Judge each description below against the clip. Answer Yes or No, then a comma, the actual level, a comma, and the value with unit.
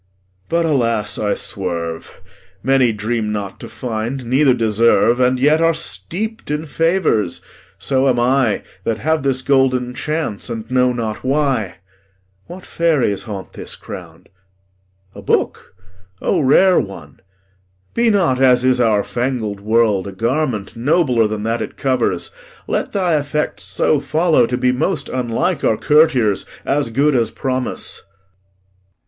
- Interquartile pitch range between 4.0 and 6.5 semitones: Yes, average, 4.8 semitones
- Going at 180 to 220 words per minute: No, average, 140 wpm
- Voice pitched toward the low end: Yes, low, 125 Hz